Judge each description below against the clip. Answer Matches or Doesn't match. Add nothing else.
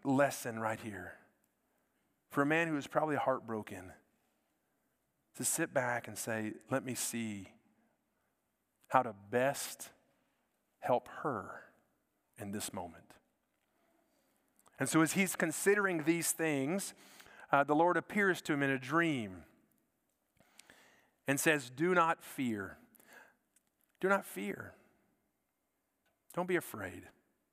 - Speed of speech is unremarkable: Doesn't match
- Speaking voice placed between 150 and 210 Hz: Doesn't match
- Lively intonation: Matches